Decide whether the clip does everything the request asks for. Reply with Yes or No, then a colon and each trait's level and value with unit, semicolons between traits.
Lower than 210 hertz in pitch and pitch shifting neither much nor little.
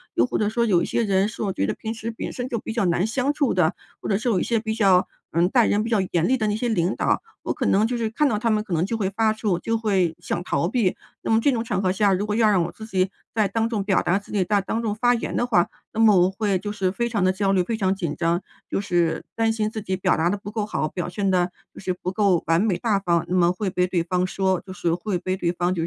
Yes: high, 200 Hz; average, 3.5 semitones